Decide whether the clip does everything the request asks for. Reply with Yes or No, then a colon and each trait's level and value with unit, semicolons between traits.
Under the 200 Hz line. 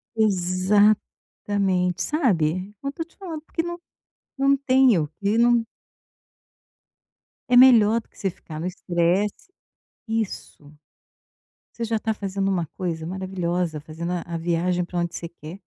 Yes: high, 190 Hz